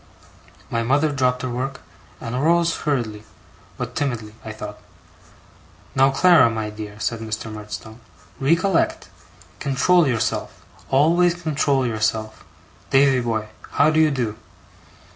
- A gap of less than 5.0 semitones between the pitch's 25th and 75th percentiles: No, average, 5.3 semitones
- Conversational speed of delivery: No, slow, 125 wpm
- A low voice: Yes, low, 130 Hz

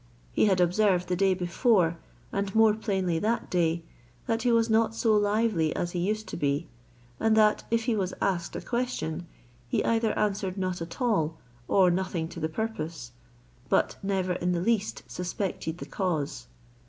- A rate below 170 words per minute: No, average, 175 wpm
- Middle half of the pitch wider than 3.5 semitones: Yes, average, 4.1 semitones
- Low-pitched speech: No, high, 190 Hz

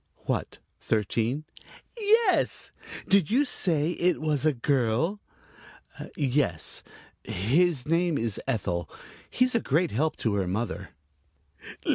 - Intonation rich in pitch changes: Yes, wide, 7.8 semitones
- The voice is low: No, medium, 145 Hz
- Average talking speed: No, slow, 105 wpm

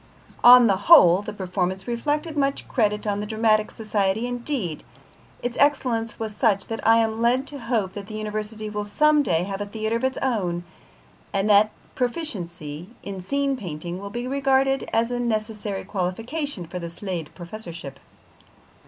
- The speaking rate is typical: Yes, average, 165 wpm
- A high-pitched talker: Yes, high, 215 Hz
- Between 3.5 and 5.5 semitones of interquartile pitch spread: Yes, average, 4.3 semitones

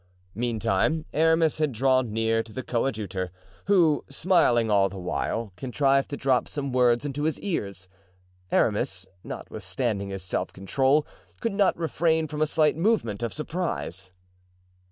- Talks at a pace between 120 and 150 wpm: Yes, average, 140 wpm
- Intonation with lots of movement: Yes, wide, 6.1 semitones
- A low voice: Yes, low, 130 Hz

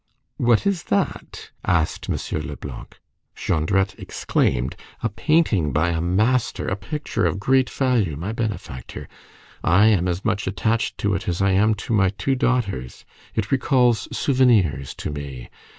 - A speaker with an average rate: Yes, average, 150 wpm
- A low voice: Yes, low, 100 Hz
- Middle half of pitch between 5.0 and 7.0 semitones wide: Yes, wide, 5.6 semitones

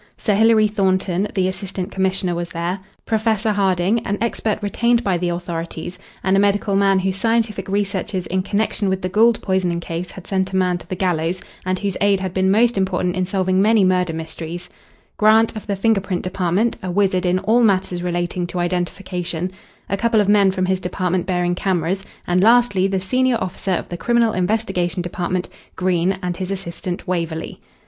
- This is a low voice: No, high, 190 Hz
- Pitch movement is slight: Yes, narrow, 2.2 semitones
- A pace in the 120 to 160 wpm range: No, average, 185 wpm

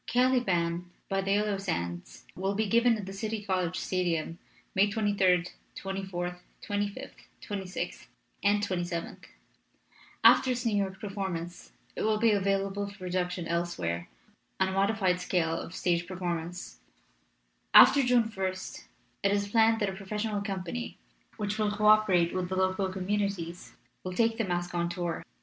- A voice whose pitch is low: No, high, 195 Hz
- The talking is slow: No, average, 150 wpm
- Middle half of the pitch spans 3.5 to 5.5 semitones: No, average, 2.7 semitones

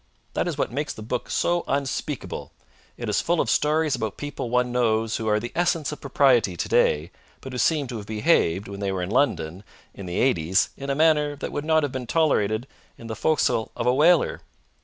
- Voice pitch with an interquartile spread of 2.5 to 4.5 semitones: No, wide, 5.6 semitones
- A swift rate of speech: Yes, fast, 215 wpm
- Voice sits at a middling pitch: No, low, 125 Hz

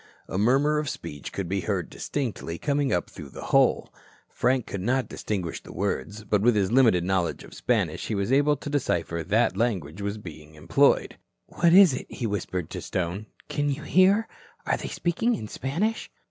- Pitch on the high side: No, low, 105 Hz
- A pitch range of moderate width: No, wide, 7.4 semitones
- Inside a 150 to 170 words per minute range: No, average, 190 wpm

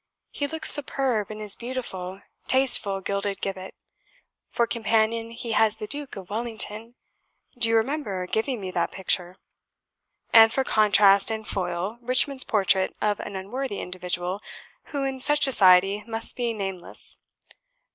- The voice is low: No, high, 215 Hz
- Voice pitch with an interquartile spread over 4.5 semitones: No, average, 3.9 semitones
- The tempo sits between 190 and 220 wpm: No, average, 145 wpm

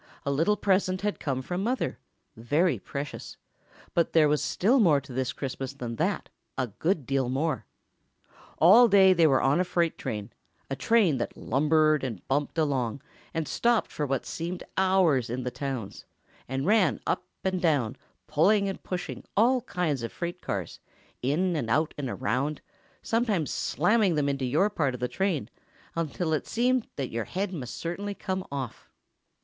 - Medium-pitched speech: Yes, medium, 155 Hz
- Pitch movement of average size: No, wide, 5.9 semitones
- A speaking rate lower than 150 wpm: No, average, 165 wpm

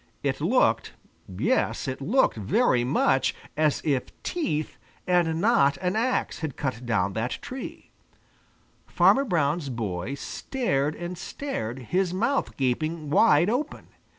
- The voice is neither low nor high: Yes, medium, 155 Hz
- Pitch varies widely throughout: Yes, wide, 6.6 semitones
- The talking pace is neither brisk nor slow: No, slow, 125 wpm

